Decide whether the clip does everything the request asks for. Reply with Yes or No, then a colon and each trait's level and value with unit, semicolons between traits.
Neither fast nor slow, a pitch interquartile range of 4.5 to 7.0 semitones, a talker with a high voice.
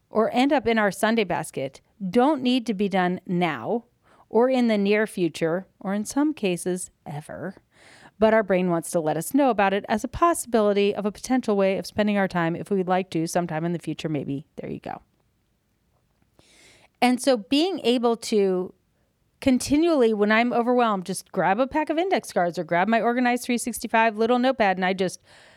Yes: average, 190 wpm; average, 4.8 semitones; high, 210 Hz